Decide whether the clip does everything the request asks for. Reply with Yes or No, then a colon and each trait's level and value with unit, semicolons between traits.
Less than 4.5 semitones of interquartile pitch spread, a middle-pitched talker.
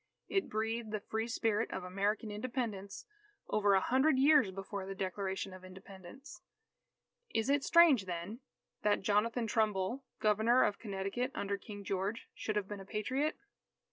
No: average, 3.3 semitones; high, 210 Hz